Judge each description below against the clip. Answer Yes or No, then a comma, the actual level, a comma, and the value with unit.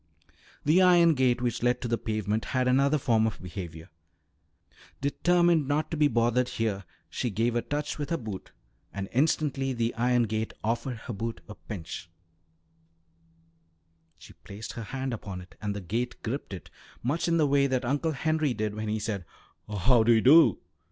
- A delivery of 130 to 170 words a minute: No, average, 180 wpm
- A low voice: Yes, low, 120 Hz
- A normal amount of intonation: Yes, average, 4.5 semitones